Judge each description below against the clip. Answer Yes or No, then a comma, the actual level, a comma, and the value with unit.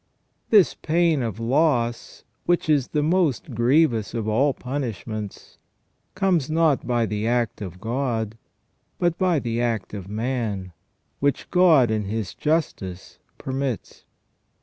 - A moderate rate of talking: No, slow, 125 wpm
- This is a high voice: No, low, 125 Hz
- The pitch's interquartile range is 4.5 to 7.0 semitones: Yes, wide, 5.6 semitones